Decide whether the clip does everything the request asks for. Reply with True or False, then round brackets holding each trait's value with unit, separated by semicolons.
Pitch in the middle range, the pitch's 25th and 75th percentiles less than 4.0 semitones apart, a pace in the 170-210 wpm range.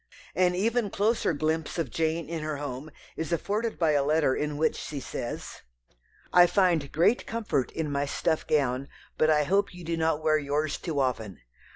True (155 Hz; 3.4 semitones; 185 wpm)